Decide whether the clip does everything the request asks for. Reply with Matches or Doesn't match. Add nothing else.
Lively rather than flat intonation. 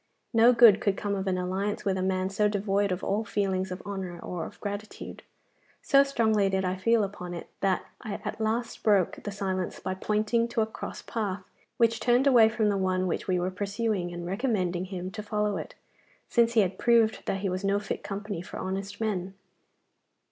Doesn't match